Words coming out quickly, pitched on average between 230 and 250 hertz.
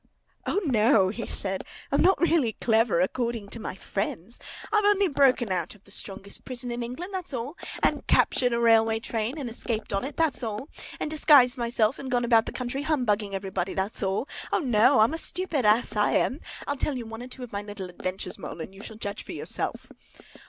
Yes: fast, 210 wpm; high, 235 Hz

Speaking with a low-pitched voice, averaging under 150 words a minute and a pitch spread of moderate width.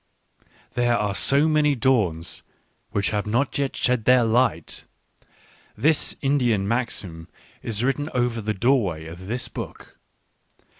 Yes: low, 120 Hz; average, 140 wpm; average, 4.5 semitones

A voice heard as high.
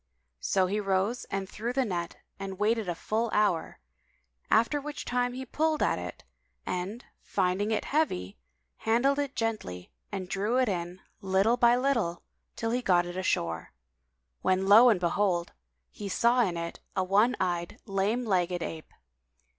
Yes: high, 200 Hz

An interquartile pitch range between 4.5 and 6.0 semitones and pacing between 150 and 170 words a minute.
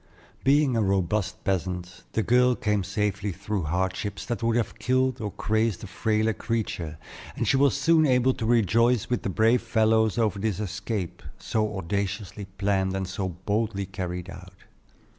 No: average, 3.3 semitones; average, 160 wpm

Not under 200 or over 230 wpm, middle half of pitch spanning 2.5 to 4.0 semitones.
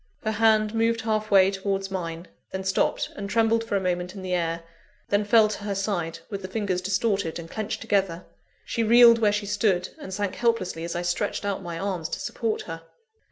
Yes: fast, 205 wpm; average, 3.0 semitones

